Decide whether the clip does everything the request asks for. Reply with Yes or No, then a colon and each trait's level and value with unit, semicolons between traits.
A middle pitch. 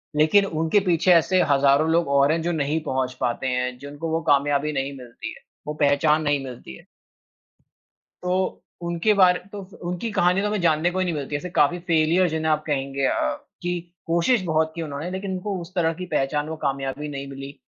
Yes: medium, 155 Hz